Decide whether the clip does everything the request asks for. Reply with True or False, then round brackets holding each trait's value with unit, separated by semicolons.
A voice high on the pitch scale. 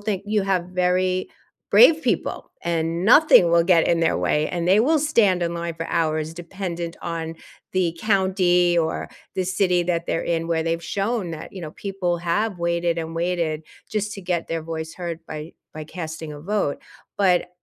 False (175 Hz)